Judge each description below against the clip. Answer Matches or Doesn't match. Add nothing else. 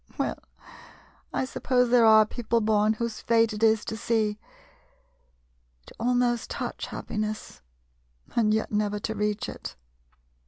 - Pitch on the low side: Doesn't match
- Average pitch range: Doesn't match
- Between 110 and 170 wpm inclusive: Matches